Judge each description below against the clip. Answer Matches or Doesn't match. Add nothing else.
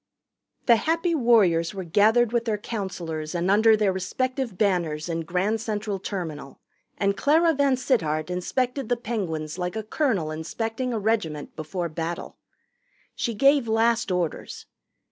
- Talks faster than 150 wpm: Doesn't match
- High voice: Matches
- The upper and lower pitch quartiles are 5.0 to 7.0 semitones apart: Matches